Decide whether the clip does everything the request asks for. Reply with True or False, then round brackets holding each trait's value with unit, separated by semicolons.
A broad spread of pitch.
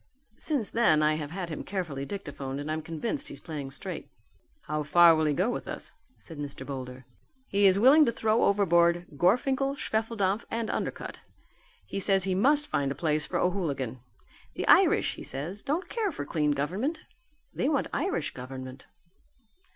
True (7.2 semitones)